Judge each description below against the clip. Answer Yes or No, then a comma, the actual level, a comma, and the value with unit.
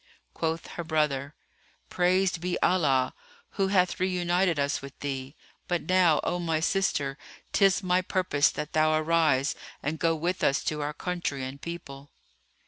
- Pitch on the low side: No, medium, 165 Hz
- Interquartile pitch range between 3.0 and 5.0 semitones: Yes, average, 3.9 semitones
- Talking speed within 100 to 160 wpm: Yes, average, 150 wpm